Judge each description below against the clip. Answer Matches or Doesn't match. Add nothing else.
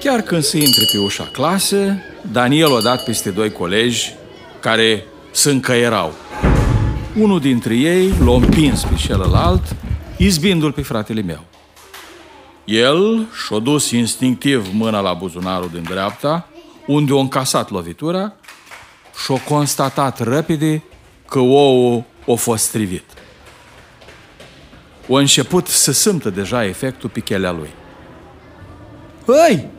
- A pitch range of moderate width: Doesn't match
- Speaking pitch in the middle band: Doesn't match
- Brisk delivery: Doesn't match